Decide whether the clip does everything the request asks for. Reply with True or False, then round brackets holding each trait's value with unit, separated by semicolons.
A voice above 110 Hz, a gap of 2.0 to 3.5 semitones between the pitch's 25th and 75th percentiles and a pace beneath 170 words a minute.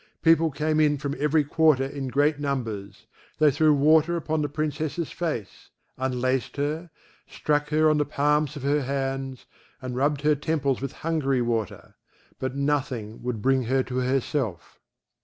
True (140 Hz; 2.6 semitones; 160 wpm)